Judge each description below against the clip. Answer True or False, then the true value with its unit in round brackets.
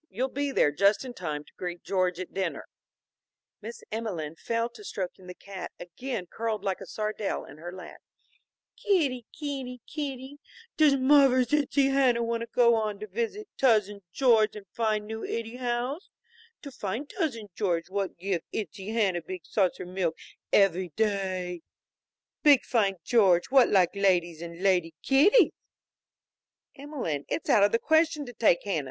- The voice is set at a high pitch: True (215 Hz)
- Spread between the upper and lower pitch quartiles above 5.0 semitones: True (5.6 semitones)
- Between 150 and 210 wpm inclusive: True (160 wpm)